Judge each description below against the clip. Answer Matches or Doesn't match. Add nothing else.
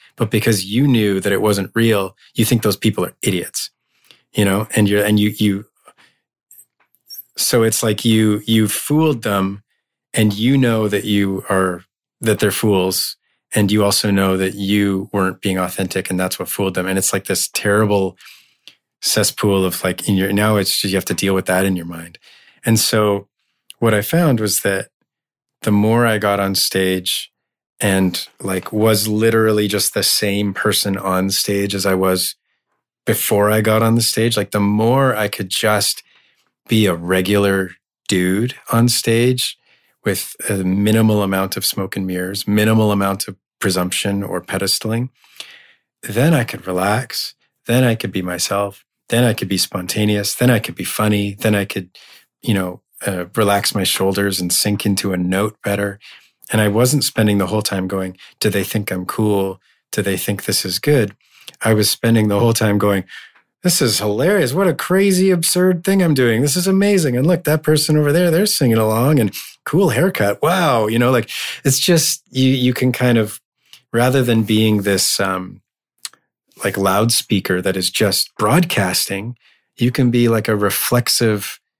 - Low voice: Matches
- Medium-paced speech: Matches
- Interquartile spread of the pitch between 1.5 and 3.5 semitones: Matches